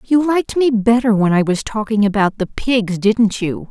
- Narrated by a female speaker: Yes, female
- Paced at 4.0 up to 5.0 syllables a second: Yes, 4.7 syllables/s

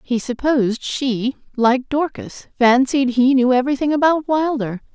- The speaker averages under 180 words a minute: Yes, slow, 135 wpm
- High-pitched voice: Yes, very high, 260 Hz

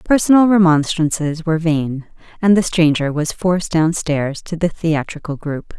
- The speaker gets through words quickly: No, average, 155 wpm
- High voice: No, medium, 165 Hz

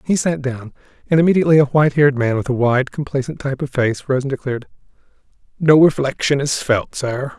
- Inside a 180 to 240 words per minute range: Yes, average, 195 wpm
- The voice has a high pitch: No, low, 135 Hz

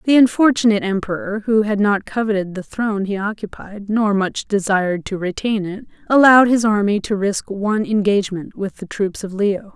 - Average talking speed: Yes, average, 180 wpm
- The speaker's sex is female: Yes, female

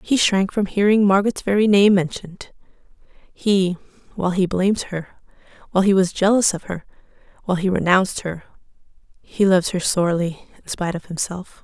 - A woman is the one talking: Yes, female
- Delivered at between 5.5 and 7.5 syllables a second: Yes, 5.8 syllables/s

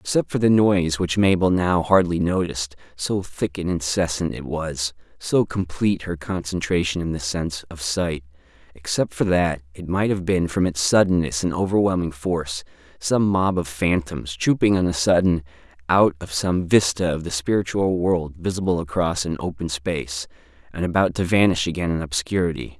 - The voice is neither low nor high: No, very low, 85 Hz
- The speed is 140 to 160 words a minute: No, average, 170 wpm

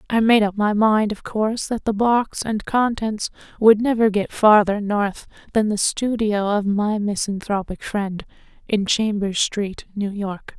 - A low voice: No, high, 210 Hz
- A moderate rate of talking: Yes, average, 165 wpm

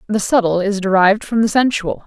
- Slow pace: No, fast, 205 wpm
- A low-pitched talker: No, high, 205 Hz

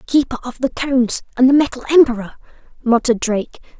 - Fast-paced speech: No, average, 175 wpm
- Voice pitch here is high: Yes, very high, 250 Hz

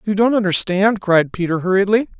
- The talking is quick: No, average, 165 wpm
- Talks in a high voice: Yes, high, 195 Hz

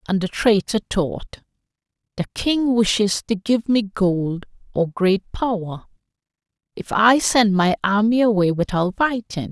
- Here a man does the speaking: No, female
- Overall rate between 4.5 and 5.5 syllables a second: No, 4.1 syllables/s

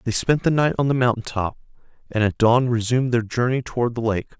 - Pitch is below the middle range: Yes, low, 120 Hz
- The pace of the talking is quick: Yes, fast, 230 wpm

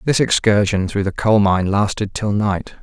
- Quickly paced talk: No, average, 190 wpm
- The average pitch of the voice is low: Yes, low, 105 Hz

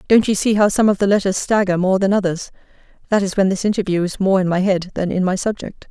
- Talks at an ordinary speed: No, fast, 255 wpm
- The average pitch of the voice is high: Yes, high, 195 Hz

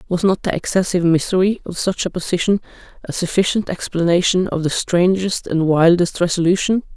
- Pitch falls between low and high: Yes, medium, 180 Hz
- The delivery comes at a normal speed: Yes, average, 155 wpm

